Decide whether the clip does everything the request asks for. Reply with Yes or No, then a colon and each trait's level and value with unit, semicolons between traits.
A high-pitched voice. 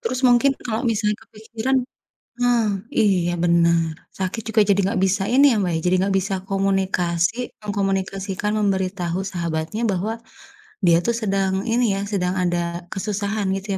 Yes: high, 195 Hz